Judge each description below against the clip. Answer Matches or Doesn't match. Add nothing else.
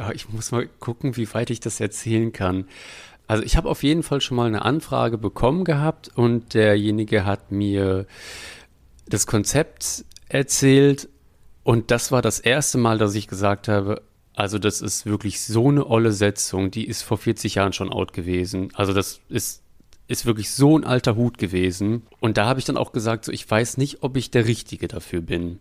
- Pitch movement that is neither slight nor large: Matches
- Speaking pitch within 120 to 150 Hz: Doesn't match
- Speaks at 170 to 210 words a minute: Matches